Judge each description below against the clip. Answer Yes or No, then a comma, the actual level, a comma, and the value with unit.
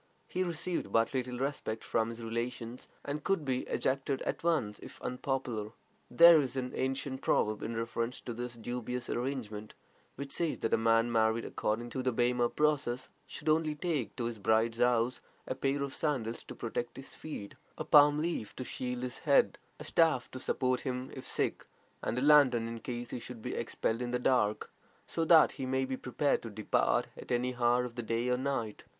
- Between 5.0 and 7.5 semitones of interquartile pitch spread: No, average, 2.8 semitones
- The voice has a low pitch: Yes, low, 125 Hz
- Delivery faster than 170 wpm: Yes, average, 195 wpm